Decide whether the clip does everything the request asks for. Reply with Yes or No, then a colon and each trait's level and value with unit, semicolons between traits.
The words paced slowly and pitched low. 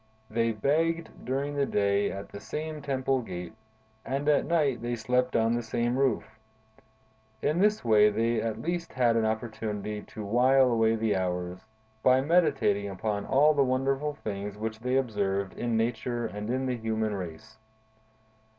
No: average, 160 wpm; low, 115 Hz